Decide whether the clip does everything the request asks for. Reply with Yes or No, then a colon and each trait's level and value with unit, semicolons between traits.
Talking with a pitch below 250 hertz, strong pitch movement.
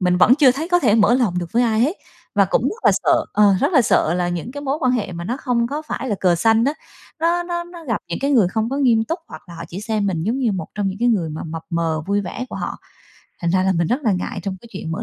Yes: high, 220 Hz; wide, 6.6 semitones